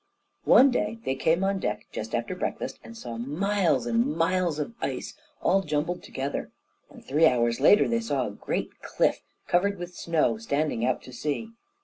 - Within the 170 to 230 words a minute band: Yes, average, 175 wpm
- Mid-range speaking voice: Yes, medium, 160 Hz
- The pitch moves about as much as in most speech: No, wide, 6.6 semitones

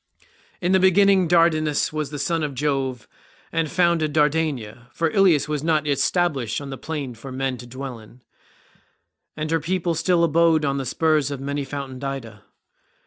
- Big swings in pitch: No, average, 3.5 semitones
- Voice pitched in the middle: Yes, medium, 150 Hz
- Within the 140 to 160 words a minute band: No, average, 175 wpm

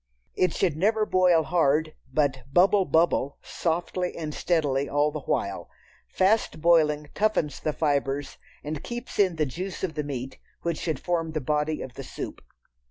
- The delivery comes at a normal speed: Yes, average, 165 wpm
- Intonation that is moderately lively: Yes, average, 3.5 semitones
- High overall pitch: No, medium, 155 Hz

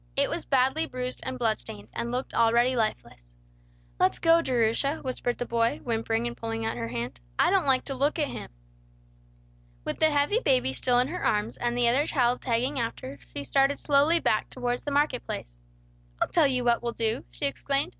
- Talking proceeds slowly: No, average, 200 wpm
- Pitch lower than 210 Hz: No, very high, 250 Hz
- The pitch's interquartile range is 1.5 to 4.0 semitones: Yes, average, 3.5 semitones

